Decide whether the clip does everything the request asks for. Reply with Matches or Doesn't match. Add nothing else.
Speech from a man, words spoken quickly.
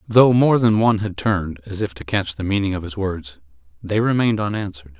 Matches